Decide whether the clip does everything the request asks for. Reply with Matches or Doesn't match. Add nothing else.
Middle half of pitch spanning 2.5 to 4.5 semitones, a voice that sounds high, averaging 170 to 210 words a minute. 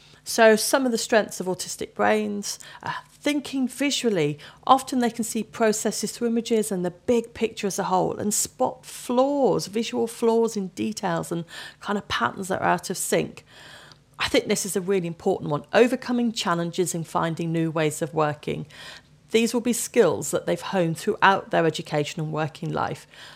Doesn't match